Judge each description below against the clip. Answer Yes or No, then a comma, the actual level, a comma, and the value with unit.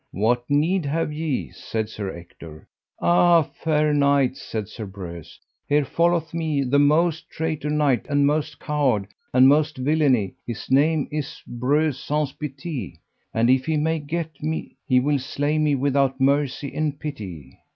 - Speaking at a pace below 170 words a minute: Yes, average, 160 wpm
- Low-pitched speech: No, medium, 145 Hz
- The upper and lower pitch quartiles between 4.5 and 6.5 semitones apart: No, average, 3.3 semitones